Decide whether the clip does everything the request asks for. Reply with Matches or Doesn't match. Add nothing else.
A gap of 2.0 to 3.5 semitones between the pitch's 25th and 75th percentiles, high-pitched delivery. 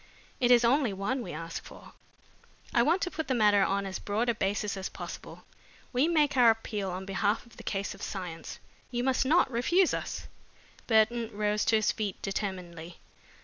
Doesn't match